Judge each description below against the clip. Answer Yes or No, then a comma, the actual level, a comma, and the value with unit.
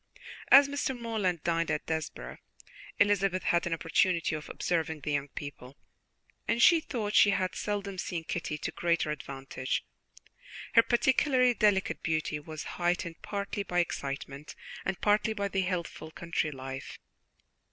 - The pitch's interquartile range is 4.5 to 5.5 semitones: Yes, average, 5.1 semitones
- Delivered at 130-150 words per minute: Yes, average, 140 wpm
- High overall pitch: No, medium, 175 Hz